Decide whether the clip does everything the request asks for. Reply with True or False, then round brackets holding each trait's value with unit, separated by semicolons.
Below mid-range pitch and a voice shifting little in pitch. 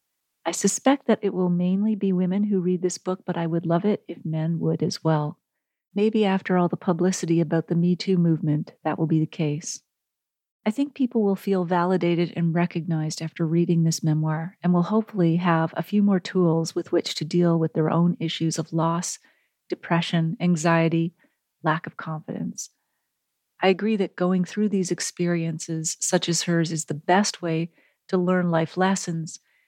False (175 Hz; 2.2 semitones)